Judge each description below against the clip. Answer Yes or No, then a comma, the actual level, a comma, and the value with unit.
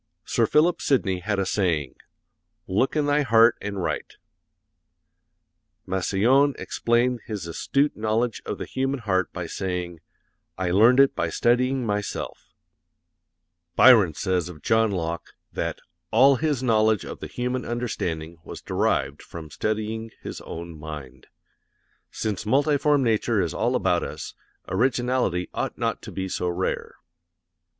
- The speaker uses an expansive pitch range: Yes, wide, 5.7 semitones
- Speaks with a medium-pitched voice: No, low, 110 Hz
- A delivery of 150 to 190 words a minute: No, slow, 135 wpm